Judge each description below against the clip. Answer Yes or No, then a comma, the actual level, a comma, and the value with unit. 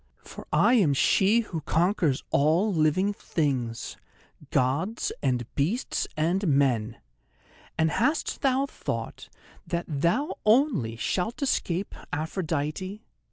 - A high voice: No, medium, 170 Hz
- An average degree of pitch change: No, wide, 6.7 semitones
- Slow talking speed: Yes, slow, 110 wpm